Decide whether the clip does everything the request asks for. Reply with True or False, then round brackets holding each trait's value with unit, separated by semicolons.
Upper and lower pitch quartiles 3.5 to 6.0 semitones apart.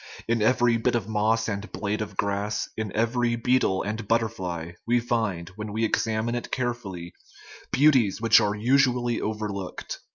False (2.6 semitones)